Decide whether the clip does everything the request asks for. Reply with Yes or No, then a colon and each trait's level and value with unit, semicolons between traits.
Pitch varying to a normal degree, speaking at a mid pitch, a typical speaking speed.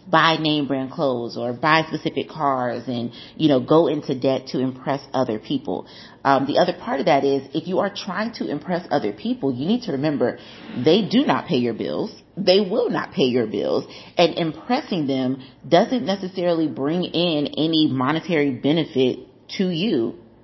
Yes: average, 4.8 semitones; medium, 150 Hz; average, 180 wpm